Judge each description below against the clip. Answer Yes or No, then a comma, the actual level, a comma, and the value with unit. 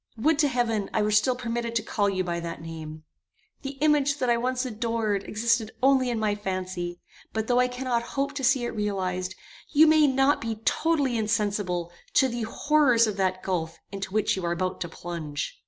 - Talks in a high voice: Yes, high, 220 Hz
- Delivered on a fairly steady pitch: No, average, 5.3 semitones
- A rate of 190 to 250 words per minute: Yes, average, 200 wpm